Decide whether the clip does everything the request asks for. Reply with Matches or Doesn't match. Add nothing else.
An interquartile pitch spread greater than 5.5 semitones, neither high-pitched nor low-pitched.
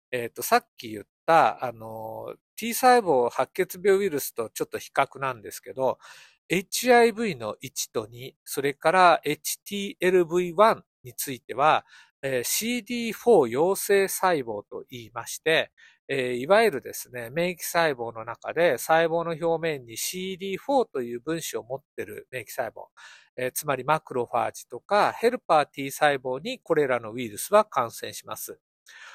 Matches